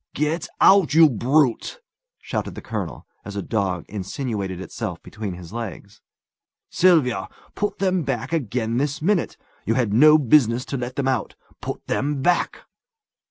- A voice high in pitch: No, low, 125 Hz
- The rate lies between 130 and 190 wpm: Yes, average, 150 wpm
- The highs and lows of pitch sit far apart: Yes, wide, 6.2 semitones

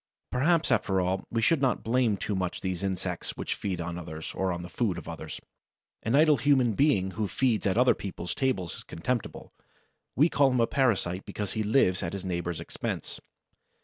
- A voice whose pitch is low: Yes, low, 100 Hz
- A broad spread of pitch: Yes, wide, 5.8 semitones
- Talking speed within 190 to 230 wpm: Yes, average, 195 wpm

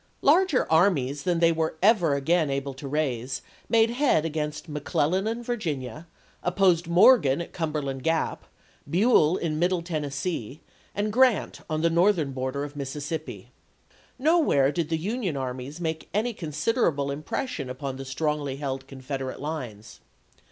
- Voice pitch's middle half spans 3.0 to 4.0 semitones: No, average, 4.7 semitones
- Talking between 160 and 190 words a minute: No, average, 150 wpm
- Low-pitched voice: No, medium, 155 Hz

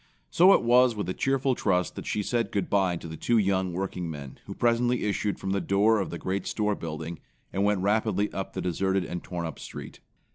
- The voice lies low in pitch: Yes, low, 100 Hz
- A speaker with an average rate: No, fast, 220 wpm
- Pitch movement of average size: Yes, average, 3.5 semitones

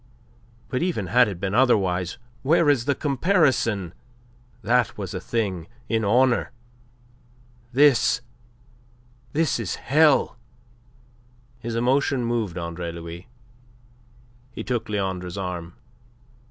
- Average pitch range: No, wide, 6.2 semitones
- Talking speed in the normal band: No, slow, 105 wpm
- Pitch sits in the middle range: No, low, 115 Hz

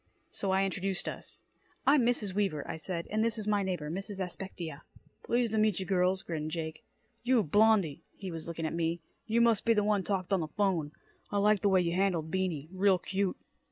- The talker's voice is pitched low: No, high, 190 Hz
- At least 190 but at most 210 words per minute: Yes, fast, 205 wpm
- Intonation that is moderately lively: Yes, average, 3.6 semitones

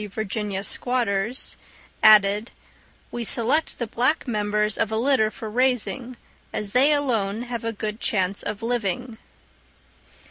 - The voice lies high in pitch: Yes, high, 225 Hz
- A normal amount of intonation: Yes, average, 3.0 semitones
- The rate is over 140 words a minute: No, slow, 135 wpm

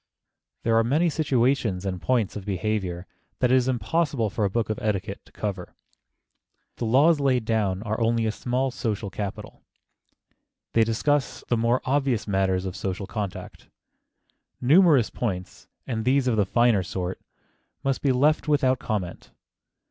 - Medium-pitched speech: No, low, 115 Hz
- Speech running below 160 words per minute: Yes, average, 150 wpm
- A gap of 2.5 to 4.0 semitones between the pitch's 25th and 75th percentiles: No, average, 4.5 semitones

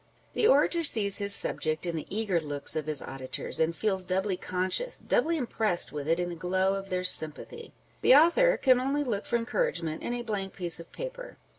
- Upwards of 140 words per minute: Yes, average, 200 wpm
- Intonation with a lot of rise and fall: Yes, wide, 7.6 semitones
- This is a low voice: No, high, 195 Hz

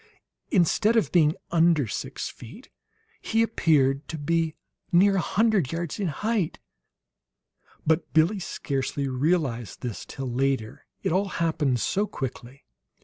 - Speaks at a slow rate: Yes, slow, 130 wpm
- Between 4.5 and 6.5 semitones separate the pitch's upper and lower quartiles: Yes, wide, 5.5 semitones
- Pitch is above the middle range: No, medium, 160 Hz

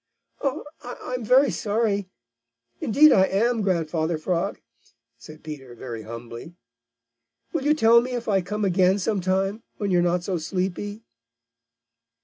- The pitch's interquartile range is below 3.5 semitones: No, average, 4.8 semitones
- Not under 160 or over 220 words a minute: No, average, 140 wpm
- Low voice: No, high, 195 Hz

